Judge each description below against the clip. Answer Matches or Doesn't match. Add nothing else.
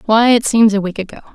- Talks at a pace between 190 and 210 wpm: Doesn't match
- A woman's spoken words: Matches